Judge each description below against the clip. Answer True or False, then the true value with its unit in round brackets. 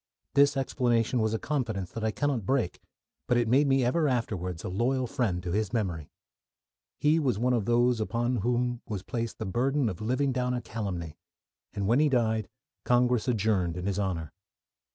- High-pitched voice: False (120 Hz)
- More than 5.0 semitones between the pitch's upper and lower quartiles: False (3.9 semitones)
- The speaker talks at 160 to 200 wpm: True (185 wpm)